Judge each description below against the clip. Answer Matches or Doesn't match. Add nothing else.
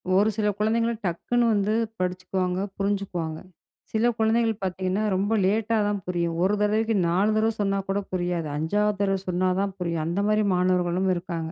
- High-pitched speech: Matches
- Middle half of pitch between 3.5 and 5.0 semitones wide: Doesn't match